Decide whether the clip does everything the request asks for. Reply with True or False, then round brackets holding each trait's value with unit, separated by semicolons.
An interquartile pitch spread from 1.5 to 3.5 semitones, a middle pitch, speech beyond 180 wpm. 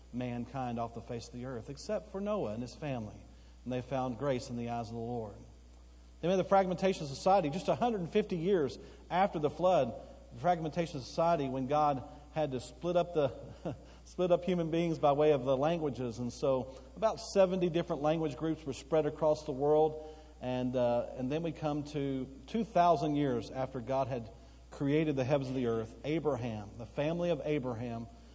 False (5.2 semitones; 145 Hz; 200 wpm)